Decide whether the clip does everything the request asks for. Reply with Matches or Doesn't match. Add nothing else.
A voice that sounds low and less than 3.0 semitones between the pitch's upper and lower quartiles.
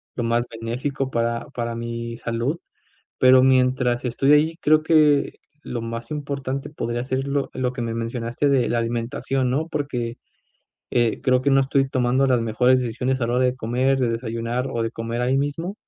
Matches